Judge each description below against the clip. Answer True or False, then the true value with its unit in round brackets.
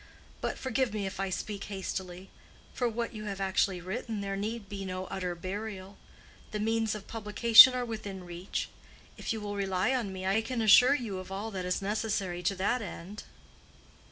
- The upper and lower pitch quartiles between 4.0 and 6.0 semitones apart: False (2.8 semitones)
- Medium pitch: False (200 Hz)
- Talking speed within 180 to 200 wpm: True (185 wpm)